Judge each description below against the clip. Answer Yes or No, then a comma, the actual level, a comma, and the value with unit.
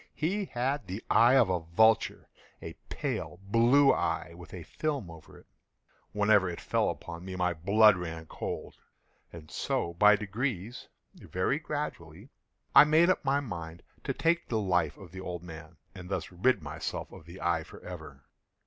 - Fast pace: No, average, 160 wpm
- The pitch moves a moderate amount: No, wide, 6.2 semitones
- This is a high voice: No, very low, 95 Hz